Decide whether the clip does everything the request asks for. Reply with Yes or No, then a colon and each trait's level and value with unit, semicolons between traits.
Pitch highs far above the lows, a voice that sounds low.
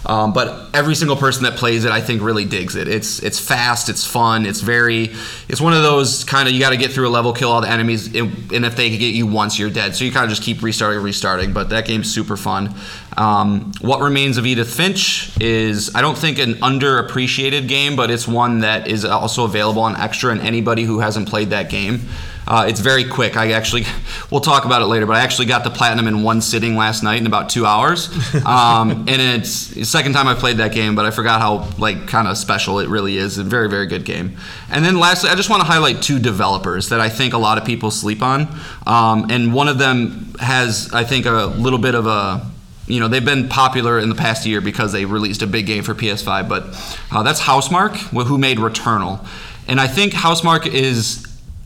No: average, 3.1 semitones; low, 115 Hz